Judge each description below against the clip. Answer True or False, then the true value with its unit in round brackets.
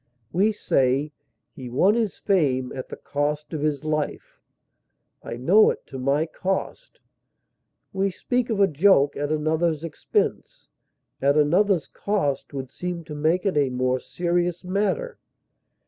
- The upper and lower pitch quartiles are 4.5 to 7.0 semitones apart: True (5.2 semitones)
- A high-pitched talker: False (155 Hz)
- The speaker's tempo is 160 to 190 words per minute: False (145 wpm)